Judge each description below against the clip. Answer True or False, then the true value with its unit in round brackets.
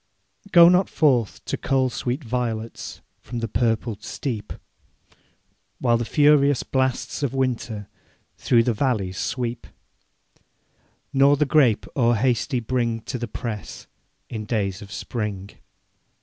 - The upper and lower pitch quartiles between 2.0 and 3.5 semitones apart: True (3.2 semitones)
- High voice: False (120 Hz)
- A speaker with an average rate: False (120 wpm)